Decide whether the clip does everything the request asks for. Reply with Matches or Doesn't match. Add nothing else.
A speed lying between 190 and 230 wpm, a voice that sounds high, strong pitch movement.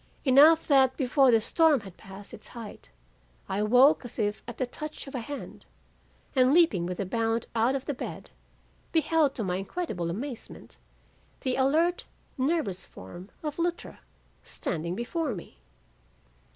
Doesn't match